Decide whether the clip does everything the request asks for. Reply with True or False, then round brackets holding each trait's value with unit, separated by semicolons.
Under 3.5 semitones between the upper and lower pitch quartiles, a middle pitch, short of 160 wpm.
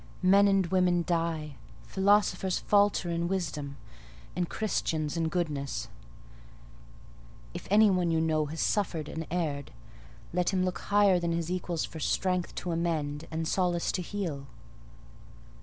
True (2.7 semitones; 170 Hz; 140 wpm)